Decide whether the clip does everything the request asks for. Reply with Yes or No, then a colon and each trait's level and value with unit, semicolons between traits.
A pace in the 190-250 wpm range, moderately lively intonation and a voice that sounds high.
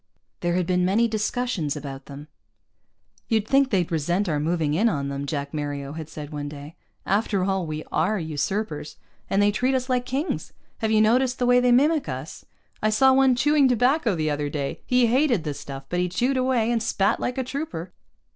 No: fast, 205 wpm; wide, 8.4 semitones; high, 195 Hz